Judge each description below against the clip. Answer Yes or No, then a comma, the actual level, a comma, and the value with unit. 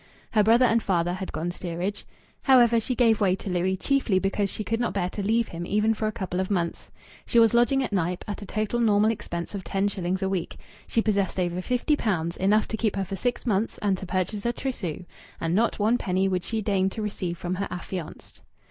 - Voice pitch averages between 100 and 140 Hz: No, high, 200 Hz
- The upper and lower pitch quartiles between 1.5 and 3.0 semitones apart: No, average, 3.5 semitones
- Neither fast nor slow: No, fast, 230 wpm